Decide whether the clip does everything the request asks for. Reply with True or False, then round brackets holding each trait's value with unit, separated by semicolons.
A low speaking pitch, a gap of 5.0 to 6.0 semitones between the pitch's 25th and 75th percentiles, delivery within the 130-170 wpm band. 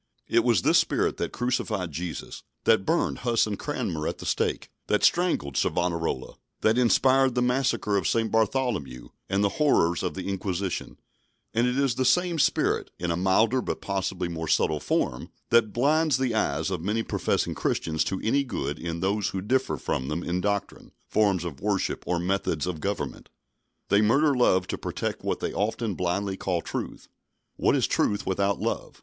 False (100 Hz; 5.4 semitones; 180 wpm)